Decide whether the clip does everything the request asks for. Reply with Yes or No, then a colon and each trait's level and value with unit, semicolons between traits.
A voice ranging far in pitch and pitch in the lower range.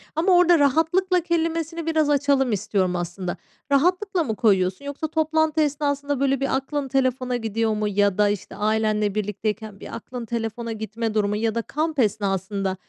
No: wide, 6.3 semitones; high, 245 Hz